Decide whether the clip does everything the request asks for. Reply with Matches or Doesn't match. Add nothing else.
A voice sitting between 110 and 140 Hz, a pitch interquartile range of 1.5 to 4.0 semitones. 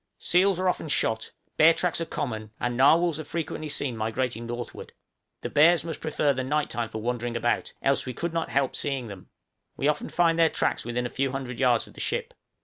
Doesn't match